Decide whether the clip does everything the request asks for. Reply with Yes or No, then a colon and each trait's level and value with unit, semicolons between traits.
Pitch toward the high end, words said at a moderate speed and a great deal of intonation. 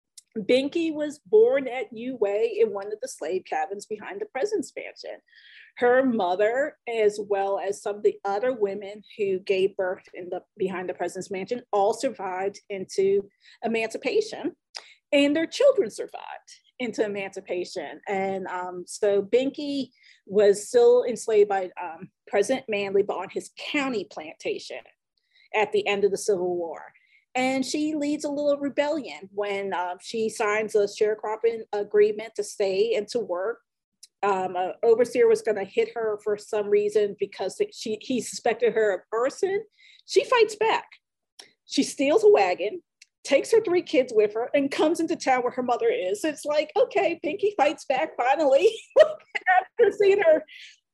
Yes: high, 240 Hz; average, 160 wpm; wide, 8.9 semitones